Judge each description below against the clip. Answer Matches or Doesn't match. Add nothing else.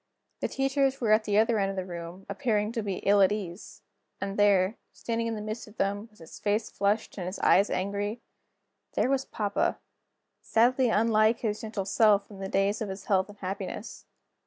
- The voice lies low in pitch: Doesn't match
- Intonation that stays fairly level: Matches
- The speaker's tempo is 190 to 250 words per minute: Matches